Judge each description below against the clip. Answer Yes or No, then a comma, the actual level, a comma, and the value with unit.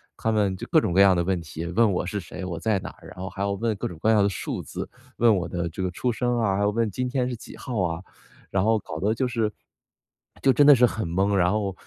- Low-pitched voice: Yes, low, 100 Hz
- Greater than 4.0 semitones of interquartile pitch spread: No, average, 3.7 semitones